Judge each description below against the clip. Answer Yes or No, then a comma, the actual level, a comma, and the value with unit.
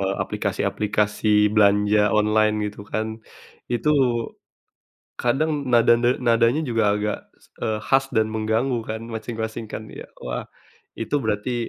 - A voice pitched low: Yes, low, 110 Hz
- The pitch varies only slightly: Yes, narrow, 2.0 semitones